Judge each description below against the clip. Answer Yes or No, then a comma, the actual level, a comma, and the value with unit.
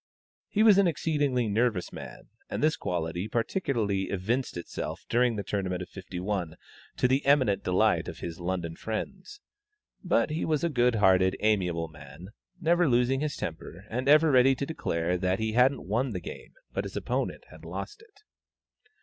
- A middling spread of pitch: No, wide, 7.4 semitones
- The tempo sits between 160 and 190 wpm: Yes, average, 170 wpm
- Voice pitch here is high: No, low, 110 Hz